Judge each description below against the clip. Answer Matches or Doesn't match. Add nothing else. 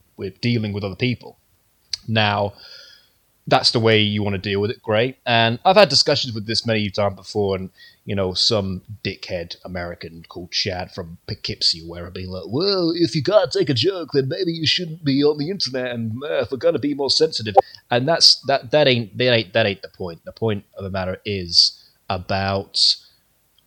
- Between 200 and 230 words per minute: Matches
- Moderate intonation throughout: Doesn't match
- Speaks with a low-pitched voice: Matches